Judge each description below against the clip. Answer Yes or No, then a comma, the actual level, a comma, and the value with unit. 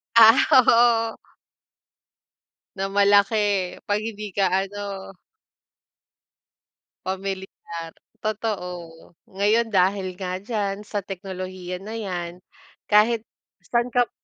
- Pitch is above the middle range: Yes, high, 200 Hz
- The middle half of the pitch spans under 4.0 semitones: Yes, narrow, 2.4 semitones